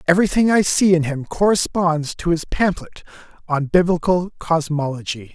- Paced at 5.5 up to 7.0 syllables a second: No, 5.1 syllables/s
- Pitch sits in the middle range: Yes, medium, 170 Hz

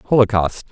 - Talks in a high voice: No, low, 105 Hz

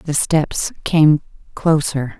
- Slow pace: Yes, slow, 110 wpm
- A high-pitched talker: No, medium, 150 Hz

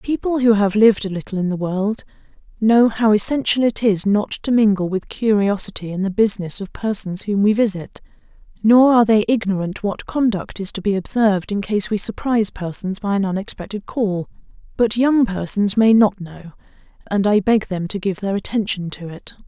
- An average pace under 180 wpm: No, average, 190 wpm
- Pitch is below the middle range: No, high, 205 Hz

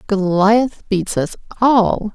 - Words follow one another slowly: Yes, slow, 110 wpm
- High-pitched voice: Yes, high, 200 Hz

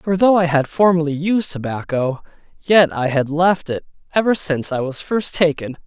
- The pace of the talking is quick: No, average, 185 wpm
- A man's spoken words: Yes, male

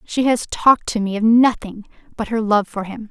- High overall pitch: Yes, high, 220 Hz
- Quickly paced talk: Yes, fast, 230 wpm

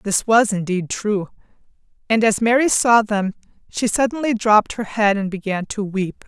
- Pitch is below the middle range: No, high, 215 Hz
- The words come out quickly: No, average, 170 wpm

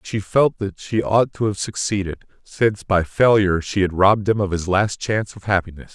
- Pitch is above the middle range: No, low, 100 Hz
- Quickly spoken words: Yes, fast, 220 wpm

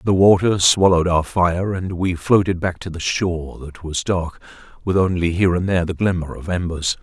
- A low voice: Yes, very low, 90 Hz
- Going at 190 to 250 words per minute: Yes, fast, 205 wpm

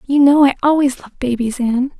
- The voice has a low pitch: No, very high, 265 Hz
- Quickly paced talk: Yes, fast, 210 wpm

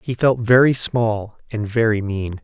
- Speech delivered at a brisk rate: No, average, 175 wpm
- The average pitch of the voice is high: No, low, 115 Hz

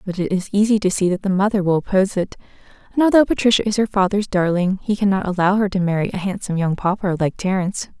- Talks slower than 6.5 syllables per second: No, 6.8 syllables/s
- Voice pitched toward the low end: No, high, 190 Hz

